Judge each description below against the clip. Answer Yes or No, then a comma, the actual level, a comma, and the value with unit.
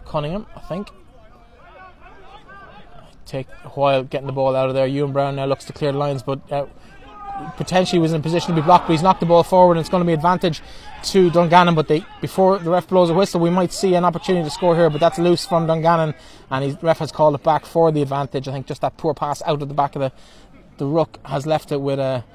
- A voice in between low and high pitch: Yes, medium, 160 Hz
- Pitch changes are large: No, average, 3.8 semitones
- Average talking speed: No, fast, 250 wpm